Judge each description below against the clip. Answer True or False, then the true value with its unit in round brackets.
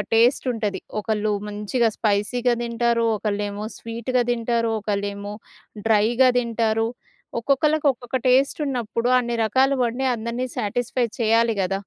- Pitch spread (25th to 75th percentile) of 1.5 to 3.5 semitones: True (2.6 semitones)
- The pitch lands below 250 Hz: True (230 Hz)